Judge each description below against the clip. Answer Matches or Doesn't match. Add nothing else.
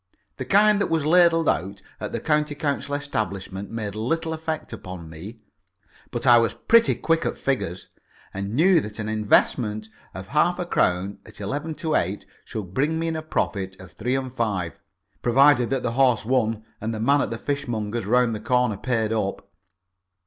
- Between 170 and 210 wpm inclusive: Matches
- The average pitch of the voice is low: Matches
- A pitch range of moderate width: Doesn't match